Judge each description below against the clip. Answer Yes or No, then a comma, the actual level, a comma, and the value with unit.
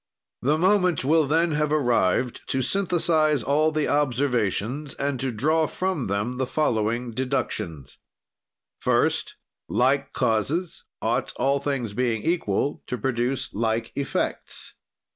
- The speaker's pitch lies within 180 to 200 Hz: No, low, 135 Hz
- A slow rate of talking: Yes, slow, 125 wpm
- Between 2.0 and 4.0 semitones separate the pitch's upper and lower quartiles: No, average, 4.6 semitones